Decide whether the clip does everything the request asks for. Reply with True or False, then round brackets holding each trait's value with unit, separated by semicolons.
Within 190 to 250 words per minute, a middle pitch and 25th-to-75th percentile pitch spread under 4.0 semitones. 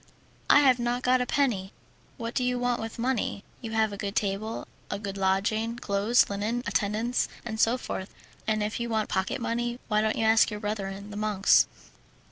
False (195 wpm; 220 Hz; 2.8 semitones)